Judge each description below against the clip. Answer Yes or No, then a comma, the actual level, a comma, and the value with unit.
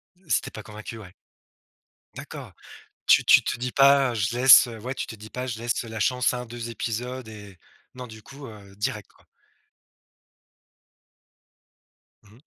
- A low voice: Yes, low, 120 Hz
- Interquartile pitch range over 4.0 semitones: No, average, 2.8 semitones